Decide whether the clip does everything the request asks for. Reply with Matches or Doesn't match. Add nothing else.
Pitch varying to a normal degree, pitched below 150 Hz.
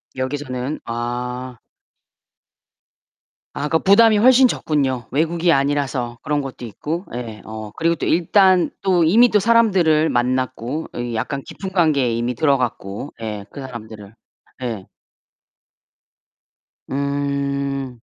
Matches